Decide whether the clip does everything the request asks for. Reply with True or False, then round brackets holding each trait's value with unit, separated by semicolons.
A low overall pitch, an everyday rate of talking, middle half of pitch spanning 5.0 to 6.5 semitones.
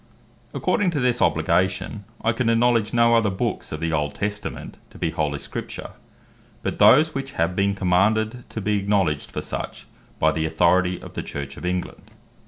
True (100 Hz; 180 wpm; 5.5 semitones)